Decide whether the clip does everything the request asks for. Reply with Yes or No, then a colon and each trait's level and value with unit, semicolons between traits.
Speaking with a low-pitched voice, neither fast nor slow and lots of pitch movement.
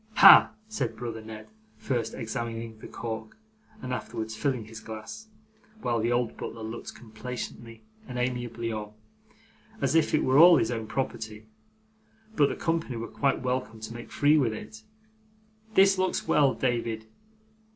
No: low, 120 Hz; average, 150 wpm; average, 3.1 semitones